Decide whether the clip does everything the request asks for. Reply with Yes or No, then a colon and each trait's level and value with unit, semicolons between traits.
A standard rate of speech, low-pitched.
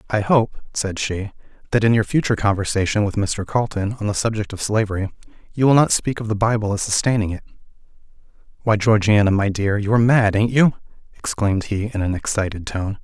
Yes: average, 195 wpm; low, 105 Hz